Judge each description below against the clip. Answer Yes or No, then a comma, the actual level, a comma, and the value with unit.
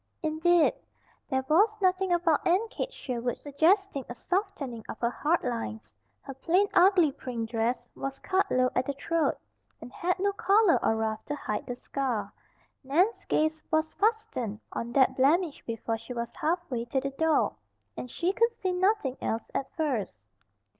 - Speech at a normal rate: Yes, average, 170 wpm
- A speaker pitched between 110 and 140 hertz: No, very high, 305 Hz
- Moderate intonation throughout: No, wide, 6.7 semitones